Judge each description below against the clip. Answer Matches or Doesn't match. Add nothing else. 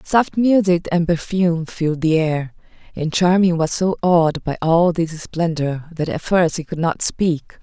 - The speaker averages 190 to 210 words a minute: Doesn't match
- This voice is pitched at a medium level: Matches